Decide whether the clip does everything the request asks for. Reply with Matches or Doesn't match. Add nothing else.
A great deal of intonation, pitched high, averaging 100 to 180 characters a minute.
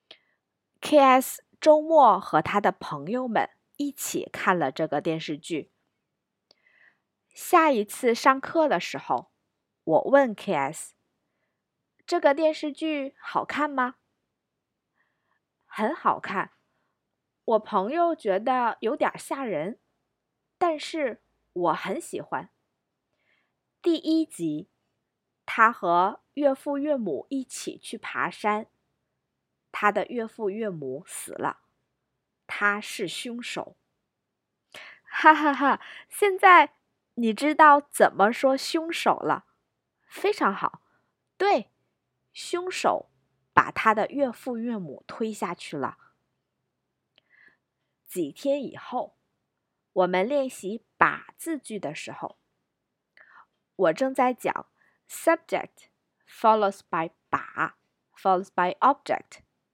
Matches